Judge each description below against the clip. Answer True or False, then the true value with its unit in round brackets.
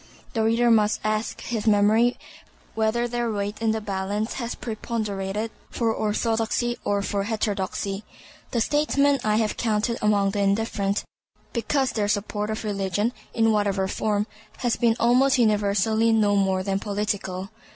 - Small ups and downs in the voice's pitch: True (2.1 semitones)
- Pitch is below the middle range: False (215 Hz)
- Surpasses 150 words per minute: False (145 wpm)